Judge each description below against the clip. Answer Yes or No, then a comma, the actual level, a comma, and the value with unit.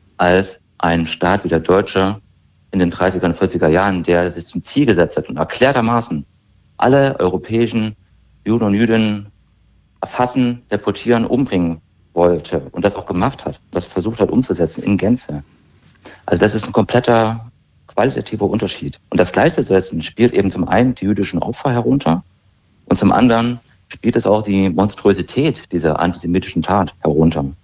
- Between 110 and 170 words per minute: Yes, average, 150 wpm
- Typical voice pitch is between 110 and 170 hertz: No, very low, 95 Hz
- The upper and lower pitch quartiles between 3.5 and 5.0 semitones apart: Yes, average, 3.8 semitones